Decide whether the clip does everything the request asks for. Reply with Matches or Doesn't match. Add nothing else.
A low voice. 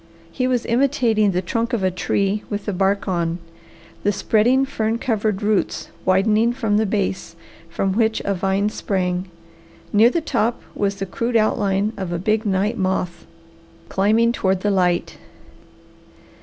Doesn't match